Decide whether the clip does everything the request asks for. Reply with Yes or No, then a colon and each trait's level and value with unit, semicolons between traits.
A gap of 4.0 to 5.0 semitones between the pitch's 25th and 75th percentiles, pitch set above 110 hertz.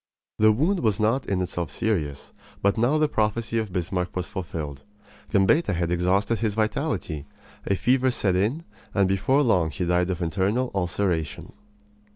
No: average, 4.4 semitones; low, 100 Hz